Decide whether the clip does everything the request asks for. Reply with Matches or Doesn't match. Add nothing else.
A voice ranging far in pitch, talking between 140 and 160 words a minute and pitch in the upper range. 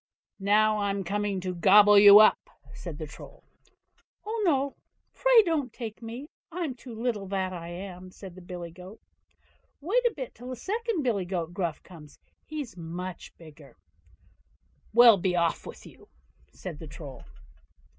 Matches